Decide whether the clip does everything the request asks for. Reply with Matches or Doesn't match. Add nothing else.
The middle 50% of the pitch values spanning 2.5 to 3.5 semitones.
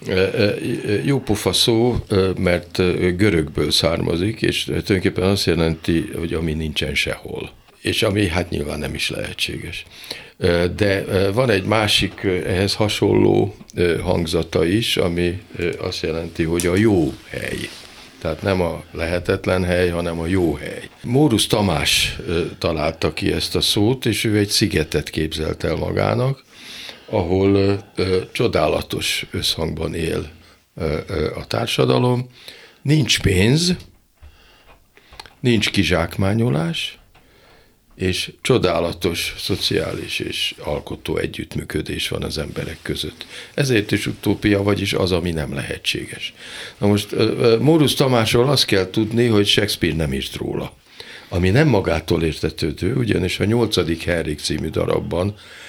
Doesn't match